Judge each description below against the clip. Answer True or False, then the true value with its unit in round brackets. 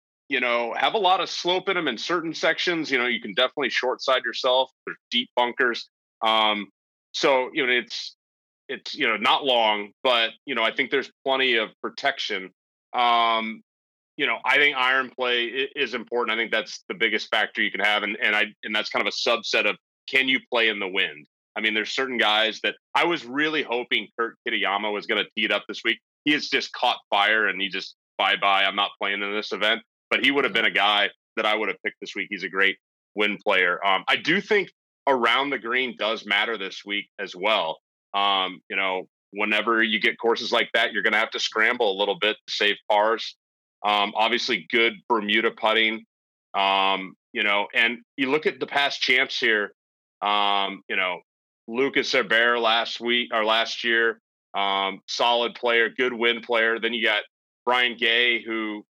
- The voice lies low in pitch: True (110 Hz)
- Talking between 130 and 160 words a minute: False (205 wpm)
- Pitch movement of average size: True (3.3 semitones)